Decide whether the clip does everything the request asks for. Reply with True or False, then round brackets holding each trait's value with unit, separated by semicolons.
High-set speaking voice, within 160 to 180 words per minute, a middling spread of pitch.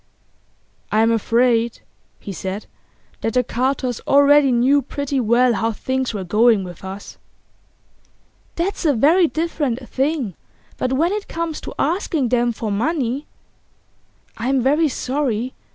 False (255 Hz; 135 wpm; 4.1 semitones)